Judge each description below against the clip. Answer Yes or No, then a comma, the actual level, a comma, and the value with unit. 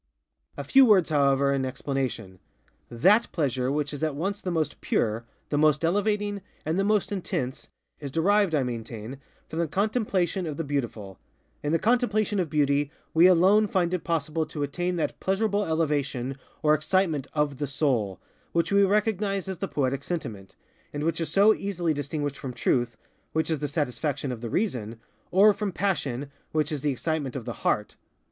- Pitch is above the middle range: No, medium, 155 Hz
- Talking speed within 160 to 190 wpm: Yes, average, 180 wpm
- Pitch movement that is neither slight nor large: No, wide, 5.7 semitones